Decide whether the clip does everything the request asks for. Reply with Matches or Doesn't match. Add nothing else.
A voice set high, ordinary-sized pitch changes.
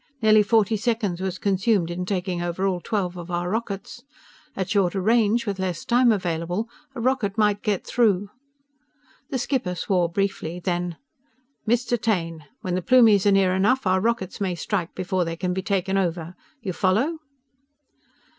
Matches